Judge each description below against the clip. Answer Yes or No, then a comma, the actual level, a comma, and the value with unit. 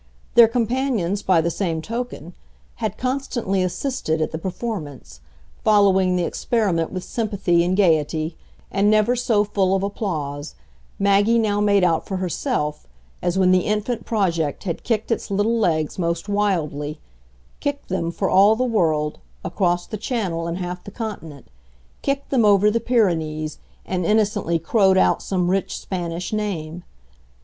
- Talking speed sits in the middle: Yes, average, 150 wpm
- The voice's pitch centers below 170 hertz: No, high, 190 Hz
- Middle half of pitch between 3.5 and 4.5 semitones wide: Yes, average, 4.2 semitones